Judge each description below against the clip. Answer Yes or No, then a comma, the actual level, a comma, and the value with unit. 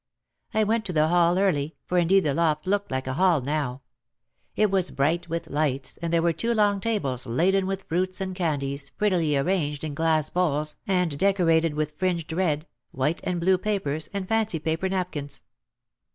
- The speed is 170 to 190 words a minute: Yes, average, 180 wpm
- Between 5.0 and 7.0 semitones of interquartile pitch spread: No, average, 4.1 semitones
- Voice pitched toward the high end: No, medium, 170 Hz